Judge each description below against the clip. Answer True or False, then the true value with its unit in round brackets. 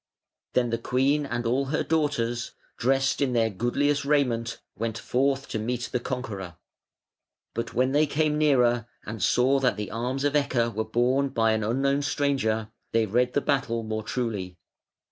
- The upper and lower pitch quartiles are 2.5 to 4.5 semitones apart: True (3.2 semitones)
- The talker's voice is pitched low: True (125 Hz)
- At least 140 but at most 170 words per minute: True (165 wpm)